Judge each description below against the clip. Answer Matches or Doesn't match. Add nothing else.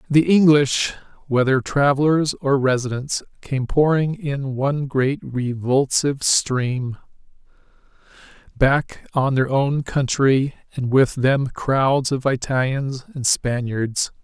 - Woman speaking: Doesn't match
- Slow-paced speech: Matches